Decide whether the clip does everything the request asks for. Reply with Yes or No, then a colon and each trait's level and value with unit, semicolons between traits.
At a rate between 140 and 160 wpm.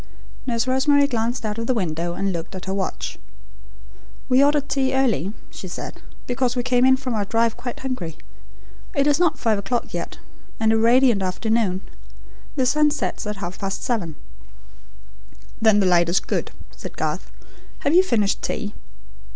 No: average, 170 wpm